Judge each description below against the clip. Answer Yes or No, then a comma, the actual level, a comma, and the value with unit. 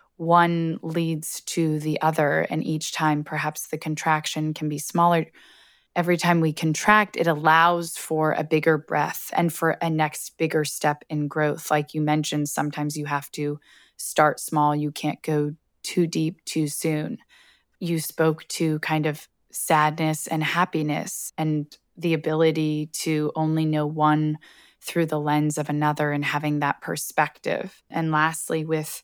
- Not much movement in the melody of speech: Yes, narrow, 1.2 semitones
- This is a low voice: No, medium, 155 Hz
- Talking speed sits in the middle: Yes, average, 155 wpm